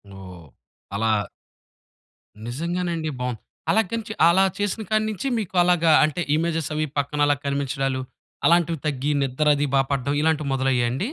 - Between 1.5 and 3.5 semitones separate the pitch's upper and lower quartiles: No, average, 4.2 semitones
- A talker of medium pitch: Yes, medium, 150 Hz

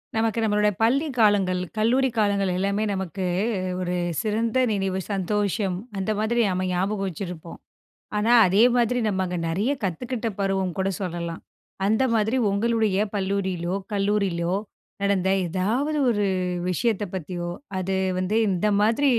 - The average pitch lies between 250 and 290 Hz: No, high, 200 Hz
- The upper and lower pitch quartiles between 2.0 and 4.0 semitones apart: Yes, average, 2.9 semitones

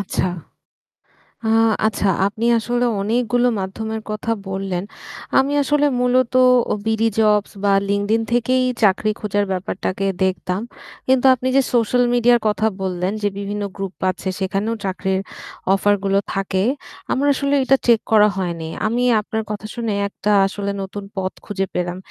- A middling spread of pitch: Yes, average, 3.6 semitones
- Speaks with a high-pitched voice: Yes, high, 210 Hz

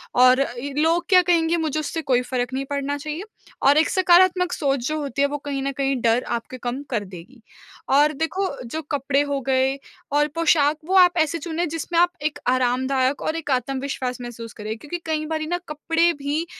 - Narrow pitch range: No, average, 3.7 semitones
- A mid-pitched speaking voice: No, very high, 285 Hz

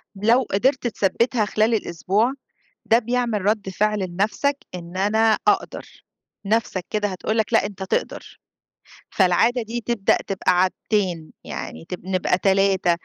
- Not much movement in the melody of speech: No, average, 3.3 semitones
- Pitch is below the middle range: No, high, 210 Hz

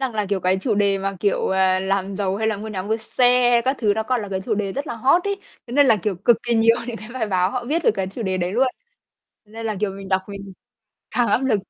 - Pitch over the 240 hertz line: No, high, 215 Hz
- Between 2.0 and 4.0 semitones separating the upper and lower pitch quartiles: Yes, average, 3.6 semitones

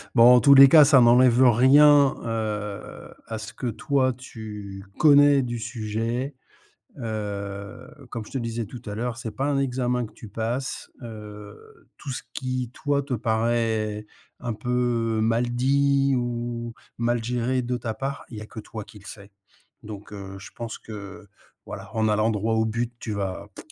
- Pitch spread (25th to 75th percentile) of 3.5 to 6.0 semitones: No, average, 2.9 semitones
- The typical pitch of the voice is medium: No, low, 115 Hz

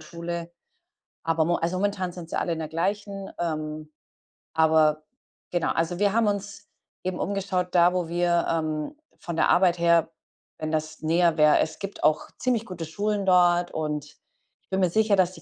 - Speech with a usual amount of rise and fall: Yes, average, 3.0 semitones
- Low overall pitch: No, medium, 175 Hz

